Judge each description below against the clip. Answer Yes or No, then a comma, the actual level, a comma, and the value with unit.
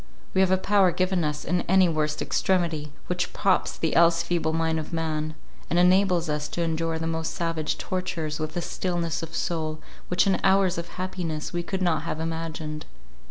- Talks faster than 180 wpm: Yes, average, 190 wpm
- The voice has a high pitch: No, medium, 165 Hz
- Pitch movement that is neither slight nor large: No, narrow, 2.3 semitones